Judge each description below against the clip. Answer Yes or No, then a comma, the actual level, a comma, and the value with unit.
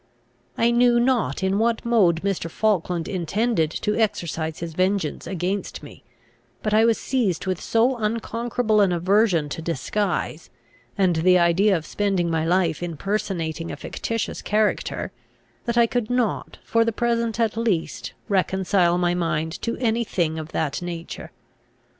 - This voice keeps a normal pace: Yes, average, 155 wpm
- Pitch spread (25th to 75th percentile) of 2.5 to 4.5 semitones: No, average, 5.0 semitones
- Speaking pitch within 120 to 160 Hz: No, high, 195 Hz